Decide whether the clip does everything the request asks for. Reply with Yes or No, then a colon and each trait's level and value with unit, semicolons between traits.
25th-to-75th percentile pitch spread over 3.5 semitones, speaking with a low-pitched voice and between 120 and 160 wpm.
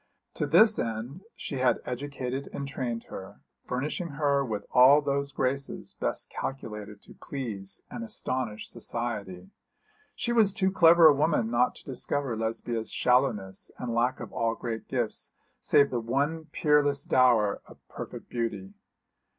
Yes: average, 3.9 semitones; low, 130 Hz; average, 145 wpm